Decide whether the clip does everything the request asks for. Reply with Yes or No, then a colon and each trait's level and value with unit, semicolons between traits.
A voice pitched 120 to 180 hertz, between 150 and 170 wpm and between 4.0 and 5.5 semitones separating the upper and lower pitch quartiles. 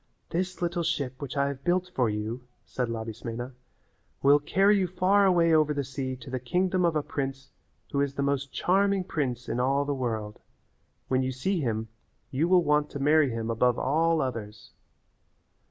No: medium, 140 Hz; average, 185 wpm; average, 5.1 semitones